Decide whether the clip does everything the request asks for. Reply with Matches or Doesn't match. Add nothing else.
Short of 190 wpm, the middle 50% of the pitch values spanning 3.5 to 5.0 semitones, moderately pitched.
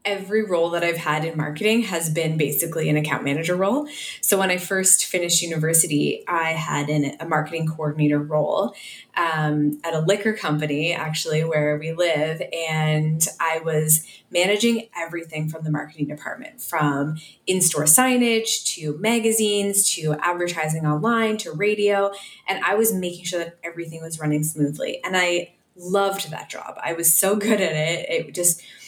Matches